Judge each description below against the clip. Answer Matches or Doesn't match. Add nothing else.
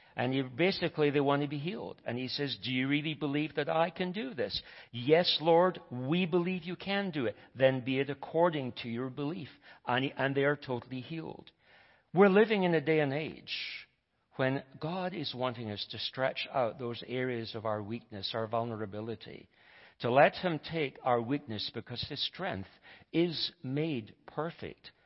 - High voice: Doesn't match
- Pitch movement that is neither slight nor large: Matches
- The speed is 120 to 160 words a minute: Doesn't match